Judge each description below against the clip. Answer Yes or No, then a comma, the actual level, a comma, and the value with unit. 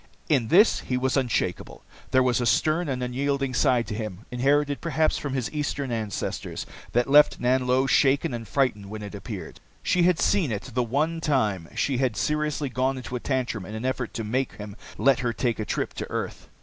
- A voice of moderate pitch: No, low, 130 Hz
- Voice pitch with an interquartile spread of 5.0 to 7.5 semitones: No, average, 3.5 semitones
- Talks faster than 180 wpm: Yes, average, 200 wpm